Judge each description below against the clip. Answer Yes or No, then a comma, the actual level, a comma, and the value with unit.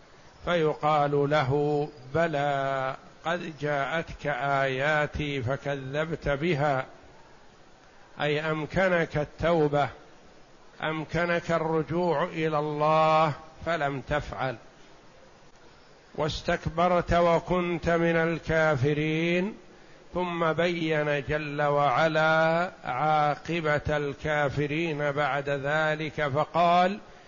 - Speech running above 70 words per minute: No, slow, 65 wpm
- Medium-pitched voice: Yes, medium, 155 Hz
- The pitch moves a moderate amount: No, narrow, 2.3 semitones